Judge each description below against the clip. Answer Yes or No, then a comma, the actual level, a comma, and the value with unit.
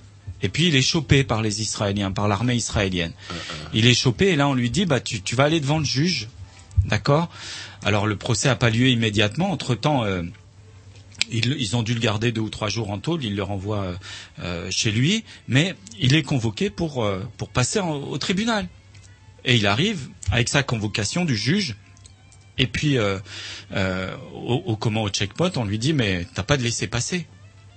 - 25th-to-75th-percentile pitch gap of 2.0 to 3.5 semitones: No, average, 5.3 semitones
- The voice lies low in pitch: Yes, low, 110 Hz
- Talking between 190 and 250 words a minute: Yes, average, 200 wpm